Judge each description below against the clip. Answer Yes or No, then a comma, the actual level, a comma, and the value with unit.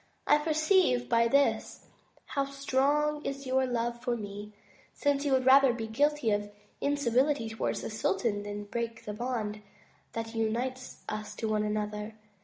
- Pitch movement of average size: Yes, average, 4.3 semitones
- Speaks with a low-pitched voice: No, high, 240 Hz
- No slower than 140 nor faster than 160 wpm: Yes, average, 155 wpm